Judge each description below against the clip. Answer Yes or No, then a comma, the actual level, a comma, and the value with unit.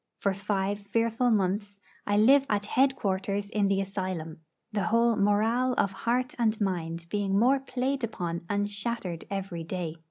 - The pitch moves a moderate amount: Yes, average, 3.1 semitones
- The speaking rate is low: No, average, 160 wpm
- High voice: Yes, high, 205 Hz